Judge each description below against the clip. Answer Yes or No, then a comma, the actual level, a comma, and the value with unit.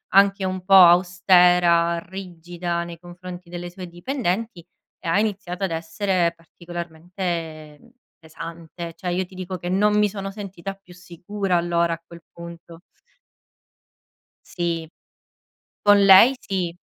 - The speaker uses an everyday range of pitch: No, narrow, 2.1 semitones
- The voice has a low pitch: No, medium, 175 Hz